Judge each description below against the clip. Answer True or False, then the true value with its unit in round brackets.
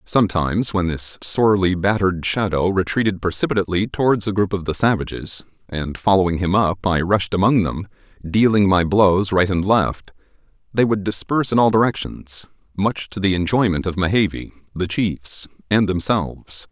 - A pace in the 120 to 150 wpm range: False (160 wpm)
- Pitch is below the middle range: True (95 Hz)